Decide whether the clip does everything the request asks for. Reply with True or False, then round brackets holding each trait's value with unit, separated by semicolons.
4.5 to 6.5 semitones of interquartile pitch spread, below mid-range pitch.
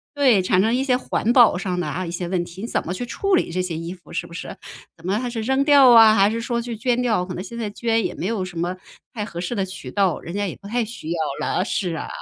False (4.8 semitones; 200 Hz)